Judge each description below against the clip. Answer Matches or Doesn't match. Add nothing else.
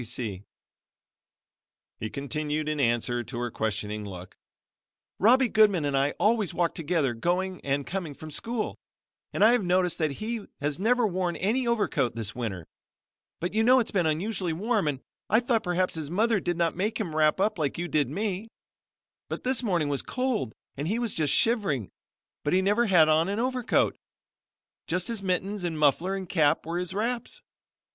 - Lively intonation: Matches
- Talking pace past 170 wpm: Matches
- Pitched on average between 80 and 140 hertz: Doesn't match